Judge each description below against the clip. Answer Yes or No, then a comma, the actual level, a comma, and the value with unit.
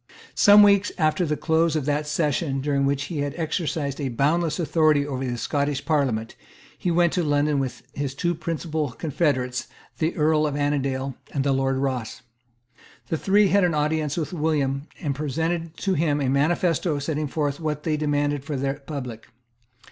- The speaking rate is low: No, average, 175 wpm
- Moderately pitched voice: Yes, medium, 150 Hz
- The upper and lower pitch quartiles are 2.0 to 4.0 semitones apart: Yes, average, 2.7 semitones